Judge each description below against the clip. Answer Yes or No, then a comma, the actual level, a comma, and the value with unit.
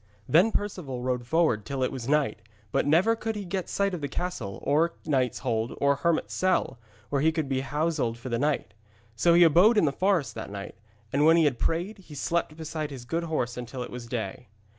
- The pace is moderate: No, fast, 215 wpm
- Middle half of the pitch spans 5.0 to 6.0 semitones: Yes, wide, 5.4 semitones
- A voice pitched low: No, medium, 150 Hz